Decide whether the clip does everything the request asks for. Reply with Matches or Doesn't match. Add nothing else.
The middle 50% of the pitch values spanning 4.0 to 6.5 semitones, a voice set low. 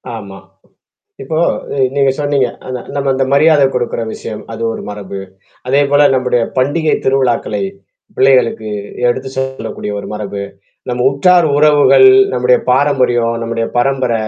Doesn't match